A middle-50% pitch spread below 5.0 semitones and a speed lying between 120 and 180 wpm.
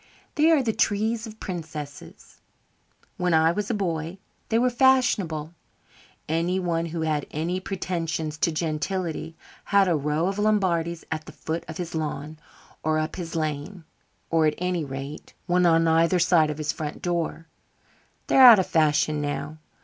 Yes: average, 3.2 semitones; average, 160 wpm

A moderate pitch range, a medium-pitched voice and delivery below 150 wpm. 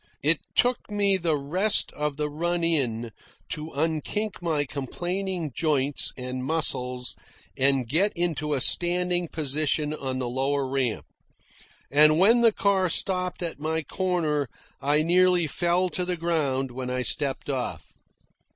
Yes: average, 4.5 semitones; medium, 155 Hz; average, 140 wpm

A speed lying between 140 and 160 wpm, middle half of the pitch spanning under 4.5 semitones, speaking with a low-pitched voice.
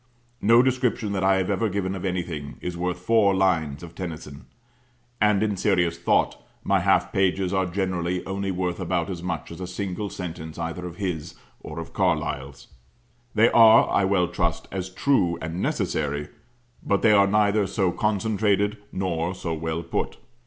No: average, 170 wpm; average, 2.9 semitones; very low, 95 Hz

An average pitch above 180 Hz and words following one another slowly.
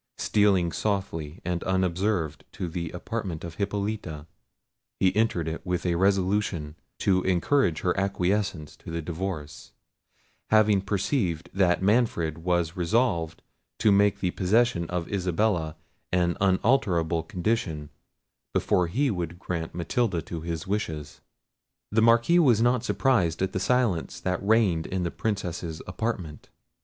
No: very low, 90 Hz; slow, 130 wpm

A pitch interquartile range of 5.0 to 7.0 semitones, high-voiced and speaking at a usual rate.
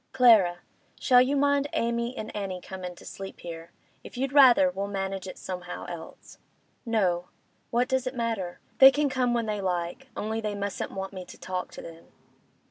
Yes: wide, 5.4 semitones; high, 210 Hz; average, 180 wpm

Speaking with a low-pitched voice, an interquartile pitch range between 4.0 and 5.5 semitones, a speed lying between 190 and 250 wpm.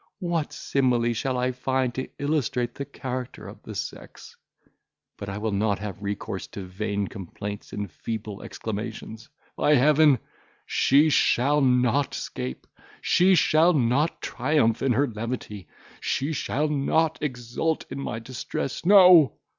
No: low, 125 Hz; average, 5.1 semitones; average, 140 wpm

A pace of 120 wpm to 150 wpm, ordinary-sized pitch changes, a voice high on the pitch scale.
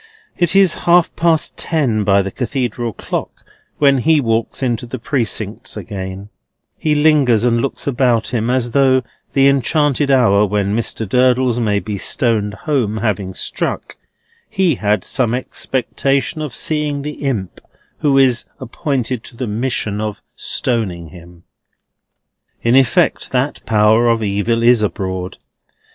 No: average, 145 wpm; average, 4.6 semitones; low, 120 Hz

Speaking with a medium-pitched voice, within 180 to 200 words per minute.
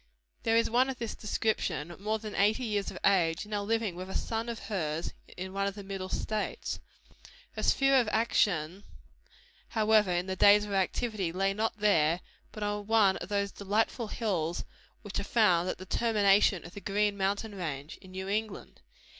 No: high, 200 Hz; average, 190 wpm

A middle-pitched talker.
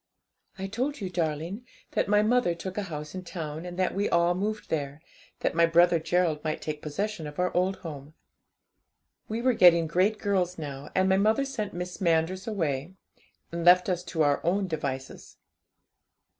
Yes: medium, 180 Hz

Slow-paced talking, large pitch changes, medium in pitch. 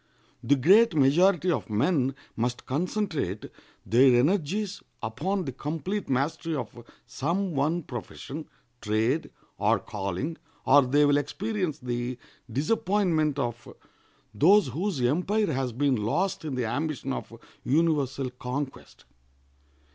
Yes: slow, 115 wpm; wide, 5.8 semitones; medium, 145 Hz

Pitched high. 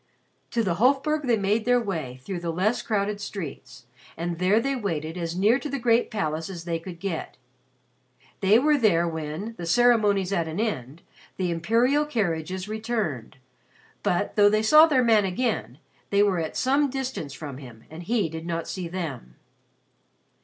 Yes: high, 195 Hz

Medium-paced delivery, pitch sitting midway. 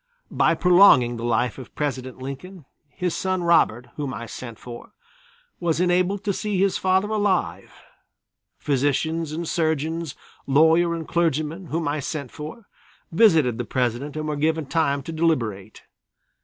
Yes: average, 145 wpm; medium, 155 Hz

